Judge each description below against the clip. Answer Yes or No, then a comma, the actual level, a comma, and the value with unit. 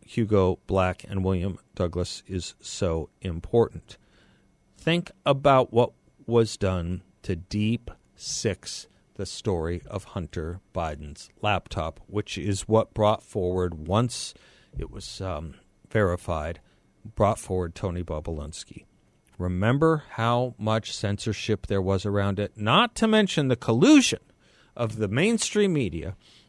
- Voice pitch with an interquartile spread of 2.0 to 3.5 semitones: No, average, 4.4 semitones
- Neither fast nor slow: No, slow, 120 wpm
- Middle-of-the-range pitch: No, low, 100 Hz